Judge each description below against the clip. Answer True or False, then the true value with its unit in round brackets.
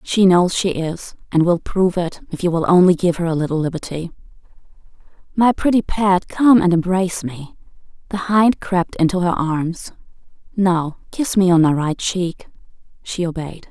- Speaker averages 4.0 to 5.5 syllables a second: True (4.8 syllables/s)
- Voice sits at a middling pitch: True (180 Hz)